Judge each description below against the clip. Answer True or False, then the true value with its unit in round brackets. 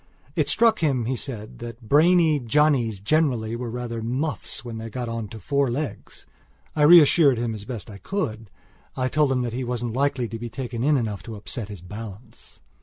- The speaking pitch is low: True (120 Hz)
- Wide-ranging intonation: False (3.9 semitones)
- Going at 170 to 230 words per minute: True (190 wpm)